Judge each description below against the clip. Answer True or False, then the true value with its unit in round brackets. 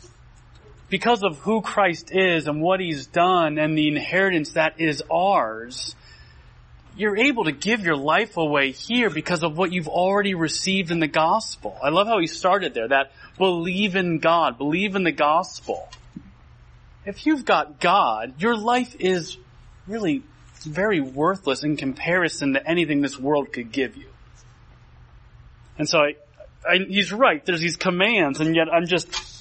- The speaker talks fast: False (160 wpm)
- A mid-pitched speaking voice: True (170 Hz)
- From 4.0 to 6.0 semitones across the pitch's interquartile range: True (4.5 semitones)